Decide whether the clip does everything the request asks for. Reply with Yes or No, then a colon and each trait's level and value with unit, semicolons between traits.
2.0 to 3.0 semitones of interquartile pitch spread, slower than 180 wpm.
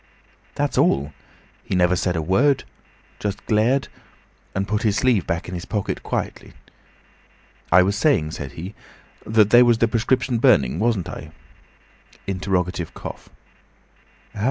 No: average, 4.5 semitones; slow, 135 wpm